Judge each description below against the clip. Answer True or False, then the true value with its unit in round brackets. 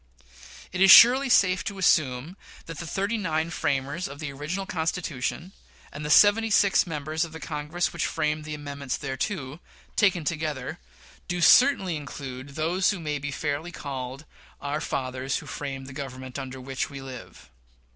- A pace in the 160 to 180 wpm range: True (165 wpm)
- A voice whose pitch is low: False (150 Hz)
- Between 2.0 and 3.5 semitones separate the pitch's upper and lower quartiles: False (4.5 semitones)